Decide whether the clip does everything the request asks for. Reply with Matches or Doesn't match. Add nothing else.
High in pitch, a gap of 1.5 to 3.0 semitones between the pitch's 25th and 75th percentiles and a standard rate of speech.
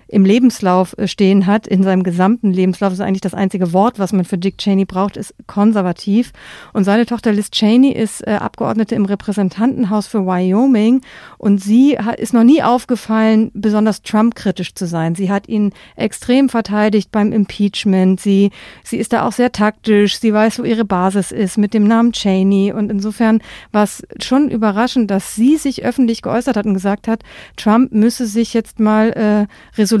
Matches